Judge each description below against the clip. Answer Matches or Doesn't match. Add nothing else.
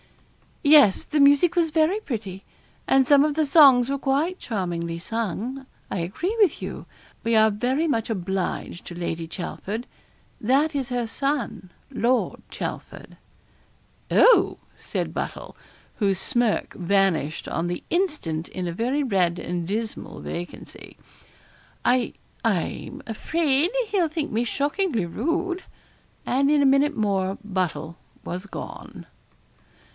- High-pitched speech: Matches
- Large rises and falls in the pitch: Matches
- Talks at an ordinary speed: Doesn't match